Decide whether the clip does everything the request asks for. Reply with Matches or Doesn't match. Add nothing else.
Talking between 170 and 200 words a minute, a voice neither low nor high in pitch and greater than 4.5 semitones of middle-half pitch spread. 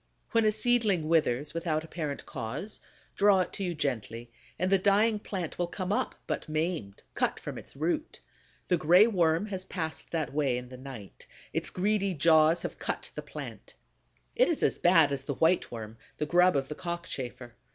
Matches